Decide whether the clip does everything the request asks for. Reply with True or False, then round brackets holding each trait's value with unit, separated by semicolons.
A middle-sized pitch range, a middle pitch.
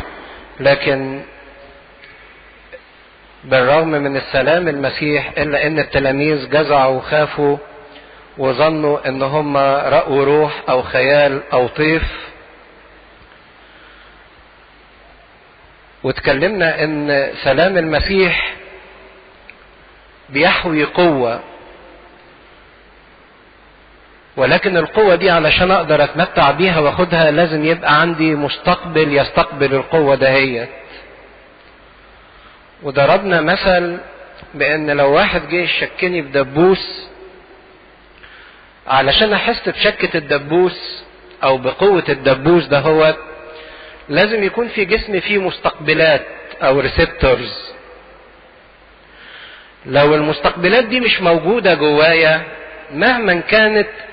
True (3.9 semitones; 155 Hz)